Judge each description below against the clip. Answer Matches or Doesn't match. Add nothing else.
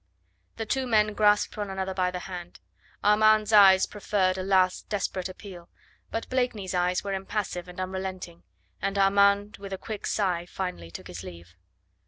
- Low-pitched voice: Doesn't match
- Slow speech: Doesn't match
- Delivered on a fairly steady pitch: Matches